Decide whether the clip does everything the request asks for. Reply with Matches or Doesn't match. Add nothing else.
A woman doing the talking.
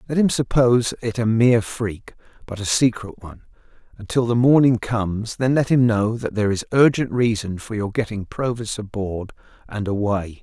Doesn't match